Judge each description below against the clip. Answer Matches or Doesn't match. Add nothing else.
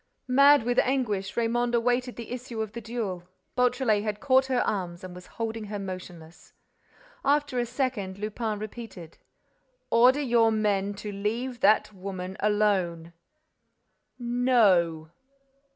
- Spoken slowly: Matches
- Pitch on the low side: Doesn't match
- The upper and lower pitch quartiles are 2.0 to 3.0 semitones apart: Doesn't match